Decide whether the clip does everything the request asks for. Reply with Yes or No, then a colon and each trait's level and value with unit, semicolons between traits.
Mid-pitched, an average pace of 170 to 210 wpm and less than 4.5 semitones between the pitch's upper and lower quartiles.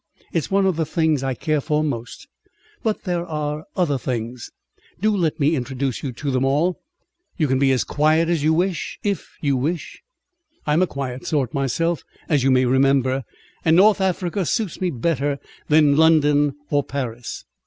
Yes: medium, 150 Hz; average, 175 wpm; average, 3.9 semitones